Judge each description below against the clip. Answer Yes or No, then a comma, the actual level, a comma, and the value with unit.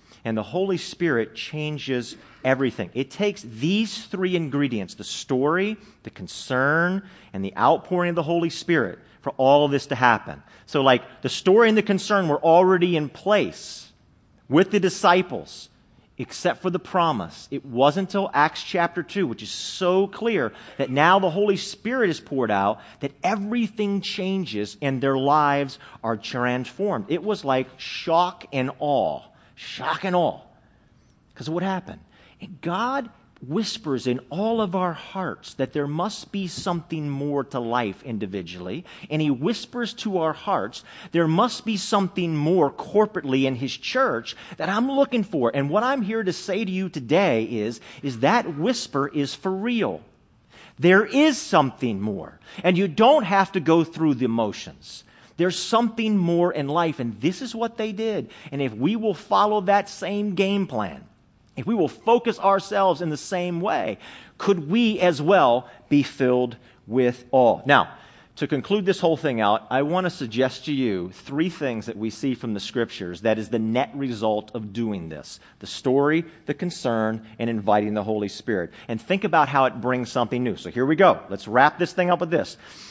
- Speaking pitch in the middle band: Yes, medium, 160 Hz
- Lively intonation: Yes, wide, 7.2 semitones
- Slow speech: No, average, 175 wpm